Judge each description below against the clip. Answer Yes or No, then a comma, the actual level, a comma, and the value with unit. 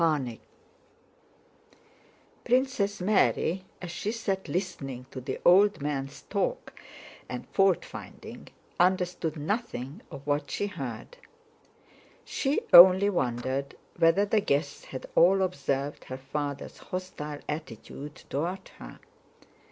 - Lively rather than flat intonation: Yes, wide, 5.8 semitones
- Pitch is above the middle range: No, medium, 170 Hz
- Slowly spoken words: Yes, slow, 110 wpm